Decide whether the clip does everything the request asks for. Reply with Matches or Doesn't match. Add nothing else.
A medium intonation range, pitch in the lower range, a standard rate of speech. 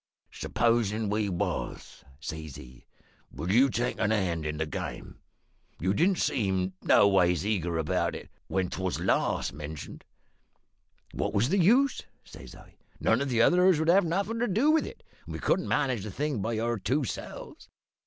Doesn't match